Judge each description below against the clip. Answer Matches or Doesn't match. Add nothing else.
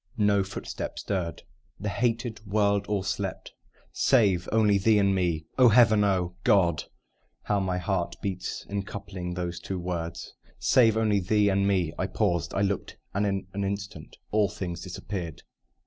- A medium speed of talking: Matches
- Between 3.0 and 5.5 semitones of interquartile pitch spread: Doesn't match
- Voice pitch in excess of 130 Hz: Doesn't match